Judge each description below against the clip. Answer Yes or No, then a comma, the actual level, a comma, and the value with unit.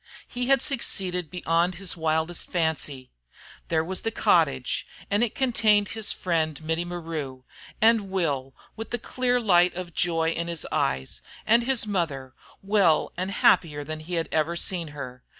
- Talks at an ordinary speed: Yes, average, 160 wpm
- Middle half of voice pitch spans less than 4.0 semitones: No, average, 4.4 semitones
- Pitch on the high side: No, medium, 175 Hz